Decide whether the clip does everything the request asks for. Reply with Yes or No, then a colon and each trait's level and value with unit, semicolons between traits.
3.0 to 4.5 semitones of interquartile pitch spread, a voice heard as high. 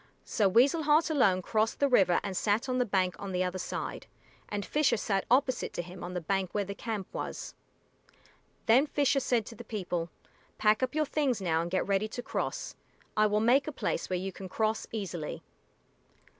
No: average, 5.1 semitones; high, 210 Hz